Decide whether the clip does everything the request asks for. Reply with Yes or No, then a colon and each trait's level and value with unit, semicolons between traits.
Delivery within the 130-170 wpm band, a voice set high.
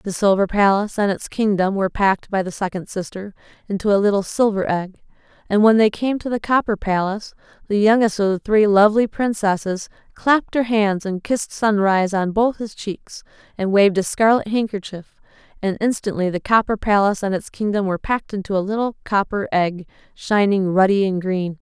No: average, 185 wpm; high, 200 Hz